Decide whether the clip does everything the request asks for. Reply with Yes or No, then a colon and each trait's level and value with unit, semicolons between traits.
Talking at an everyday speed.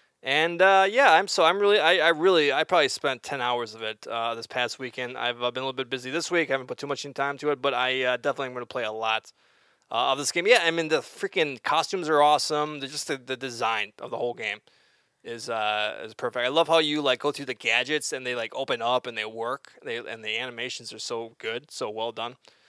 No: fast, 265 wpm